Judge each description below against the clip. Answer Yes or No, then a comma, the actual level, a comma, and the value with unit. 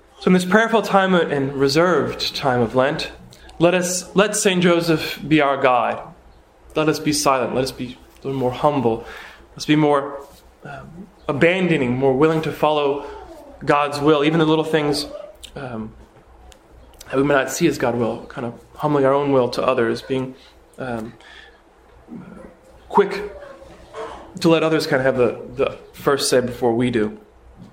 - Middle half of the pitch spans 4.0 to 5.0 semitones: Yes, average, 4.7 semitones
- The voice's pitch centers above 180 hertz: No, medium, 145 Hz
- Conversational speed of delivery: Yes, average, 165 wpm